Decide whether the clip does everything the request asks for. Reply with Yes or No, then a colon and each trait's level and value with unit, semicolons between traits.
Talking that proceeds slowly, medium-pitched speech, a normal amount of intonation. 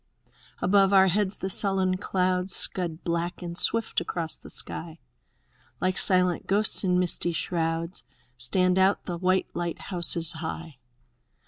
No: slow, 130 wpm; medium, 180 Hz; narrow, 2.0 semitones